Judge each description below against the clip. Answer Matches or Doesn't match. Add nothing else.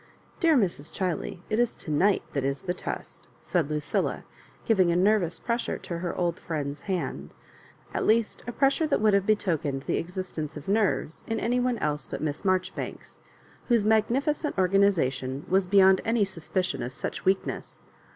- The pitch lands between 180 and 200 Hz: Matches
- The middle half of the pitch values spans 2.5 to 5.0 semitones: Doesn't match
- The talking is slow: Doesn't match